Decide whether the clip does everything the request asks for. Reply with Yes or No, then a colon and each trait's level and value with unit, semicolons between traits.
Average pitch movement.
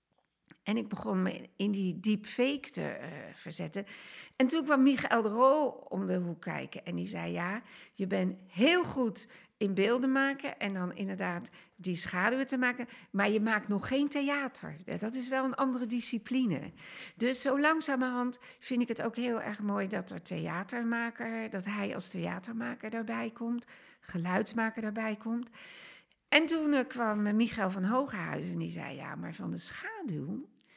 Yes: average, 4.5 semitones